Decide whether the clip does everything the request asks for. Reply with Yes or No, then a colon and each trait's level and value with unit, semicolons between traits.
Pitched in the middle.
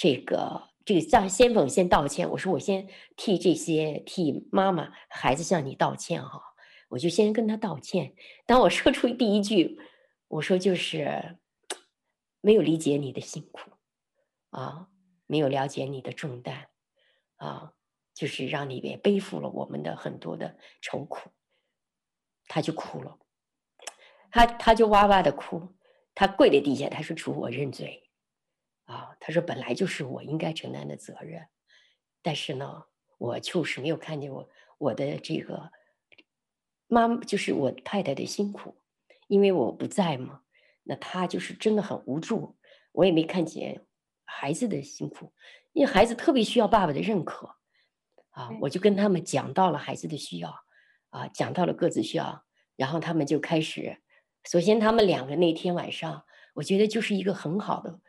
Yes: medium, 180 Hz